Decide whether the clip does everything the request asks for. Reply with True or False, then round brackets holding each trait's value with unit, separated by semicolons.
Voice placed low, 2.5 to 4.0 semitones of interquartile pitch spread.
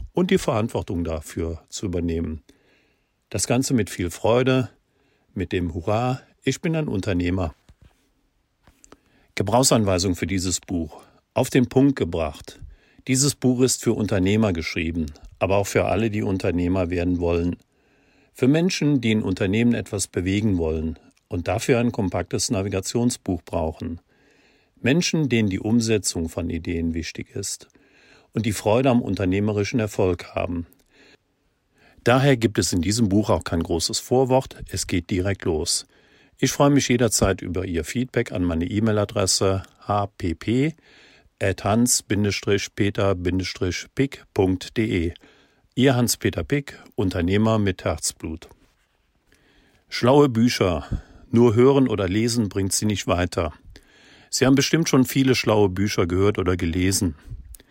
False (105 Hz; 5.2 semitones)